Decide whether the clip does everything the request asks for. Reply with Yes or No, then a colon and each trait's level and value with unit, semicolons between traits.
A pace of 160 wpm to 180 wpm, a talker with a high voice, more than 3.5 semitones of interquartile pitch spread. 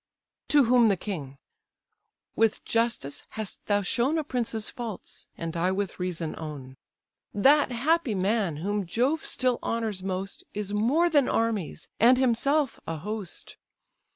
No: average, 140 wpm; high, 215 Hz; average, 5.1 semitones